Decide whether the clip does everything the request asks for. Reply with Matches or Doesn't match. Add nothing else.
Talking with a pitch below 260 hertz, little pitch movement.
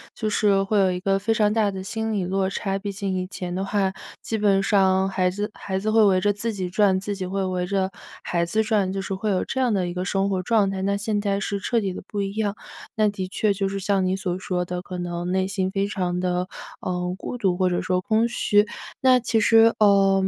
Matches